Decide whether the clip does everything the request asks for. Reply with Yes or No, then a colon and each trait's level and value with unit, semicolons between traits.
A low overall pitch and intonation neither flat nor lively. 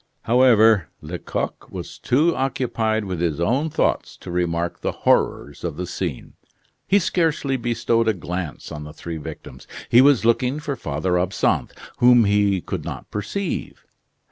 No: low, 110 Hz; wide, 6.6 semitones